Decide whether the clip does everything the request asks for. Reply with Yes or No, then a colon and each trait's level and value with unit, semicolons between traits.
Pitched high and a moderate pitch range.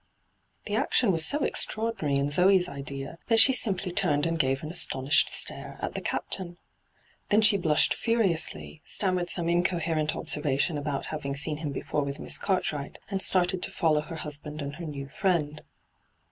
No: medium, 160 Hz; average, 4.0 semitones